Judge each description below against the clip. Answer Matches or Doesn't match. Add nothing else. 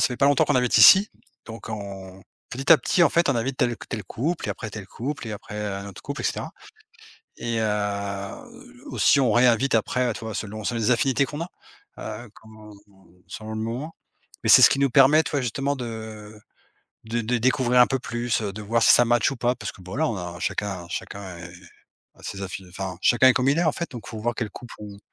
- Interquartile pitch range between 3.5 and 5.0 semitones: Matches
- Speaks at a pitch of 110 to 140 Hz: Matches